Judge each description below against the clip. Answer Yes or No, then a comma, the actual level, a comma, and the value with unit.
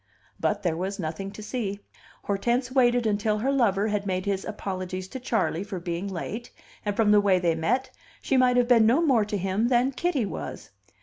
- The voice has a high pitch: Yes, high, 210 Hz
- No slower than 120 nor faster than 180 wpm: No, average, 200 wpm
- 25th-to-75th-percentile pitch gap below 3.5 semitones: No, average, 4.2 semitones